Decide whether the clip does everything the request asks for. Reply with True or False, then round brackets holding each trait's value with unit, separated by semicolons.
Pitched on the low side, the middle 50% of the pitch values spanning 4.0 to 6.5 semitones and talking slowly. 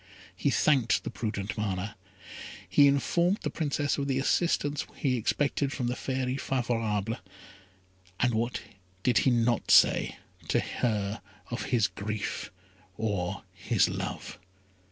True (120 Hz; 4.5 semitones; 130 wpm)